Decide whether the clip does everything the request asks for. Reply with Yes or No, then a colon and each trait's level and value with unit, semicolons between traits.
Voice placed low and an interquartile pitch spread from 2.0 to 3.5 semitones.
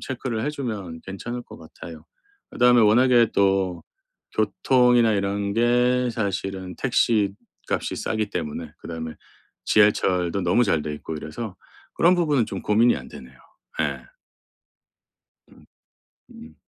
No: low, 105 Hz; wide, 5.5 semitones